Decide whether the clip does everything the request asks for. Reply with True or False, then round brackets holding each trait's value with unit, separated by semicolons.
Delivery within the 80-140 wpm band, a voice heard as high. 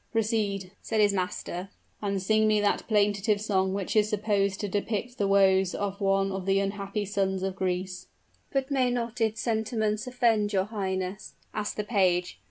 False (175 wpm; 205 Hz)